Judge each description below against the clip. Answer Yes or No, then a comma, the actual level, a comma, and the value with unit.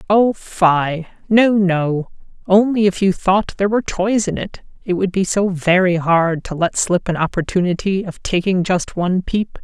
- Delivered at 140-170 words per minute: No, average, 180 wpm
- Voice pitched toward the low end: No, medium, 185 Hz